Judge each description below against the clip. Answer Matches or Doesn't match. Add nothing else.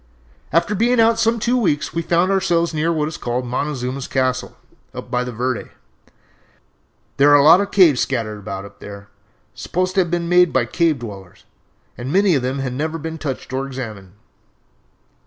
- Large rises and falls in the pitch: Matches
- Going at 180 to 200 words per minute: Matches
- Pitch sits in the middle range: Matches